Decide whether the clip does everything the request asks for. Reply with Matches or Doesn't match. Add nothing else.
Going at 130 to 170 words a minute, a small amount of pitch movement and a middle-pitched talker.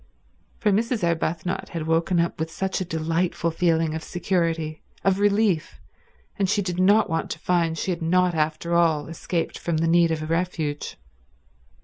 Matches